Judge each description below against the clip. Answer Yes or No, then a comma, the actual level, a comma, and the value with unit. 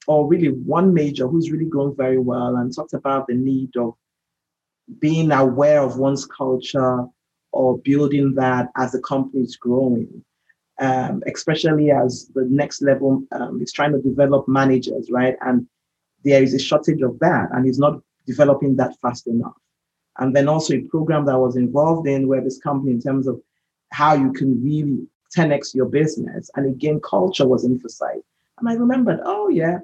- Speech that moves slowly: No, average, 175 wpm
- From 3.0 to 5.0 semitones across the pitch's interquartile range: No, narrow, 2.6 semitones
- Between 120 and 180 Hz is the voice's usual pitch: Yes, low, 135 Hz